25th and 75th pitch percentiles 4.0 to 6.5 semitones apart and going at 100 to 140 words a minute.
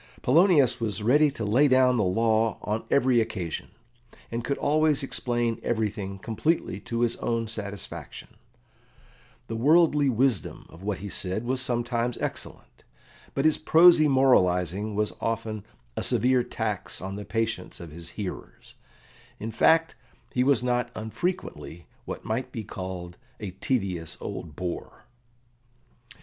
Yes: average, 4.4 semitones; slow, 135 wpm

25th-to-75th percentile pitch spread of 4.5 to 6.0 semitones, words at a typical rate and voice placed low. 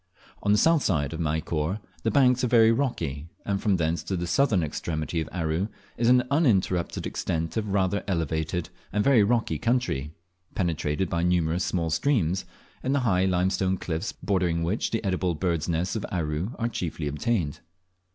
Yes: average, 5.2 semitones; average, 170 wpm; very low, 90 Hz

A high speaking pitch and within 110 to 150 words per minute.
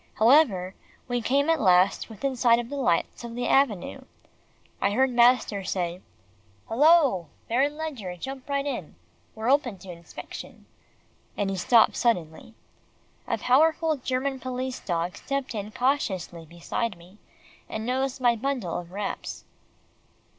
Yes: high, 235 Hz; average, 140 wpm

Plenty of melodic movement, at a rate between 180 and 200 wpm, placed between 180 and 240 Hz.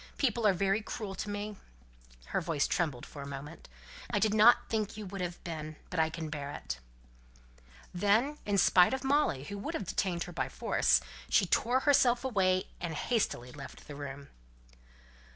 Yes: wide, 5.7 semitones; average, 185 wpm; medium, 185 Hz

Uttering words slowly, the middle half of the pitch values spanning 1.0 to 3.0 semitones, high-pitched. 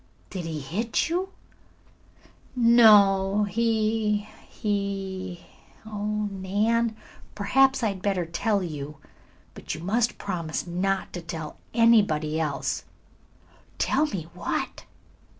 No: slow, 105 wpm; average, 4.0 semitones; high, 200 Hz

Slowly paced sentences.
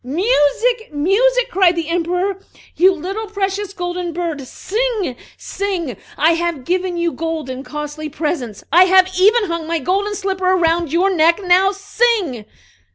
No: average, 150 wpm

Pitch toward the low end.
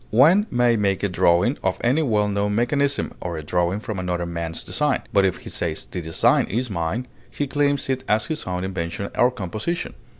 Yes: low, 105 Hz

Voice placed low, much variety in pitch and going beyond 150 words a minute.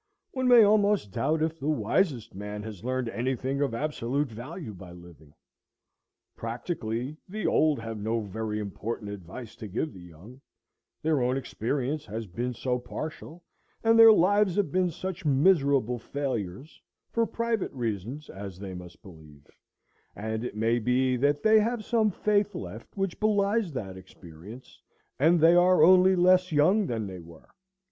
Yes: low, 130 Hz; wide, 8.7 semitones; average, 160 wpm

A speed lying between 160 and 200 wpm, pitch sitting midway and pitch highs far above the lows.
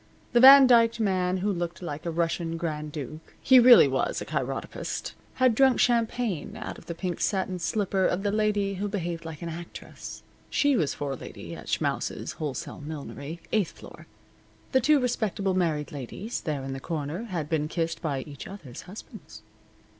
Yes: average, 175 wpm; medium, 175 Hz; wide, 5.7 semitones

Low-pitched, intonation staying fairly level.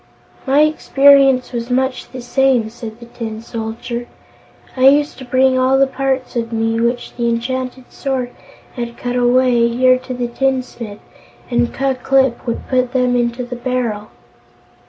No: very high, 250 Hz; narrow, 1.7 semitones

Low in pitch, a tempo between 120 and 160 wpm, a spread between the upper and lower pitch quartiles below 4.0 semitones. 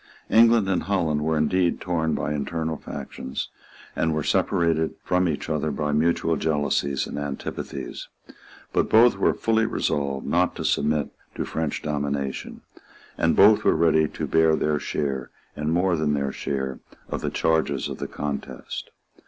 Yes: very low, 80 Hz; average, 155 wpm; narrow, 2.6 semitones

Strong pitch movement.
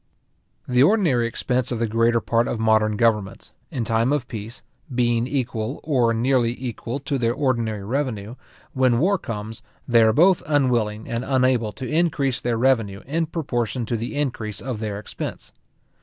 No: average, 2.8 semitones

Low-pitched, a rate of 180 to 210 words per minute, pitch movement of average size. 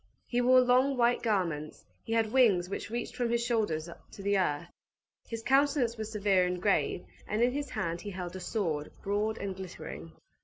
No: high, 210 Hz; average, 190 wpm; average, 4.8 semitones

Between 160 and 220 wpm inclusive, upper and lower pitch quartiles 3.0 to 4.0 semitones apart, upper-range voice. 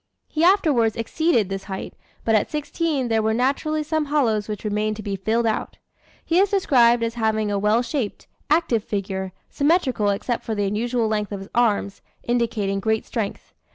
No: average, 180 wpm; average, 4.7 semitones; high, 225 Hz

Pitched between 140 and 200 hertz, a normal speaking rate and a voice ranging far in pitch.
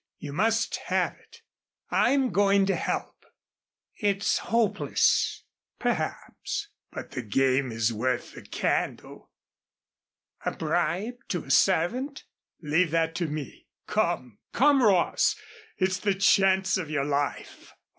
No: medium, 185 Hz; slow, 120 wpm; wide, 6.2 semitones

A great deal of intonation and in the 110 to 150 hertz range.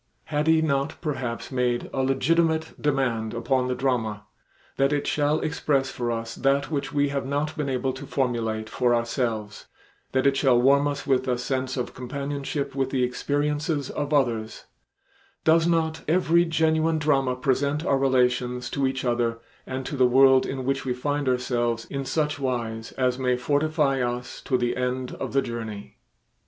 No: narrow, 2.6 semitones; low, 135 Hz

